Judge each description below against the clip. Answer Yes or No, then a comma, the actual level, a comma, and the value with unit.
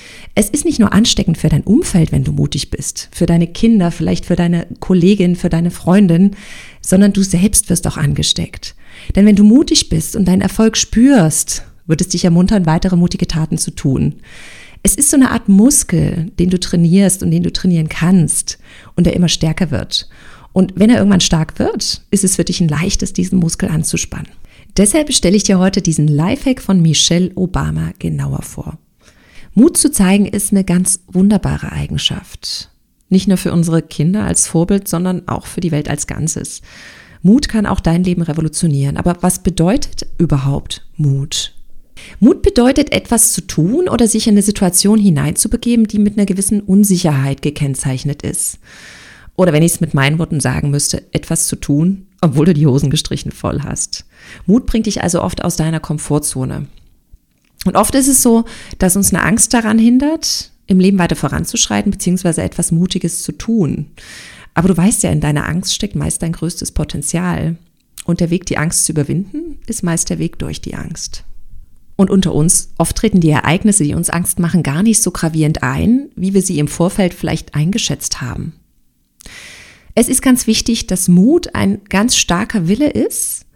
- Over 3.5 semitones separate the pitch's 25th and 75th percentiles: Yes, average, 4.2 semitones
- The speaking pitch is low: No, medium, 180 Hz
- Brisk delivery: No, average, 180 wpm